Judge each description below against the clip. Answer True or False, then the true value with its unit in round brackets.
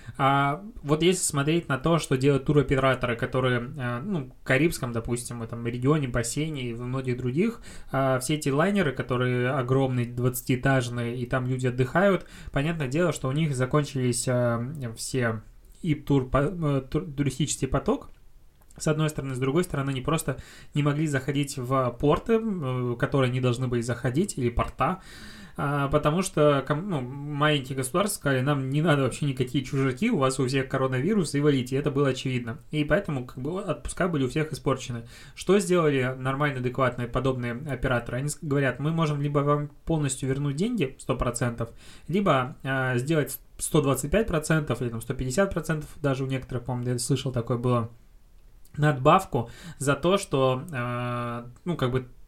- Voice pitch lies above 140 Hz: False (135 Hz)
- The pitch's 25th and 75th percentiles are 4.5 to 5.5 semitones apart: False (3.1 semitones)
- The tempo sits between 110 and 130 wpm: False (155 wpm)